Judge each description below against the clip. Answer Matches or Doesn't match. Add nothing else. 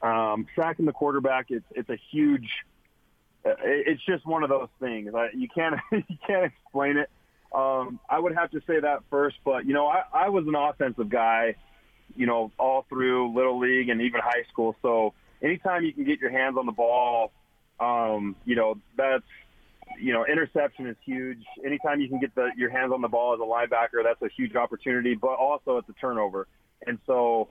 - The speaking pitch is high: Doesn't match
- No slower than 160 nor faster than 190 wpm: Doesn't match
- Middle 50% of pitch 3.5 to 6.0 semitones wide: Matches